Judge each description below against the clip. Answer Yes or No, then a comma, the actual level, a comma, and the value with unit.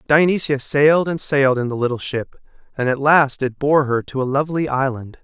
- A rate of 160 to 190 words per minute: No, fast, 205 wpm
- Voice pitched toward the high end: No, medium, 140 Hz